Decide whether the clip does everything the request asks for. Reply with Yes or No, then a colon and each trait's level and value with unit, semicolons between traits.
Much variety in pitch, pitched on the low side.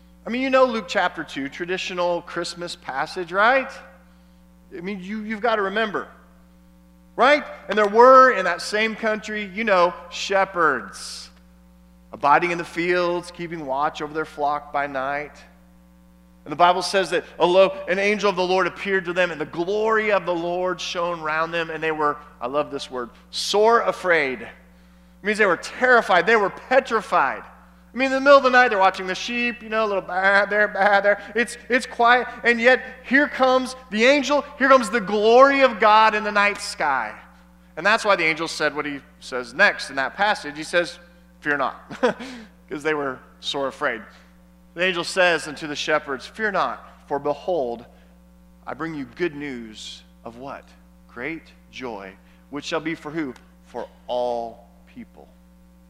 No: wide, 8.3 semitones; medium, 175 Hz